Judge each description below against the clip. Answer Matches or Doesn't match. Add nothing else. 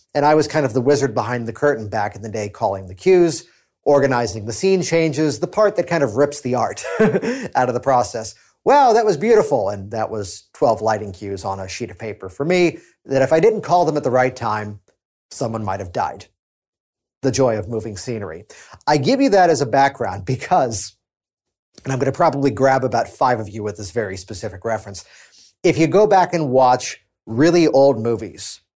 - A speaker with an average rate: Doesn't match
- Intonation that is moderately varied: Doesn't match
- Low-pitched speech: Matches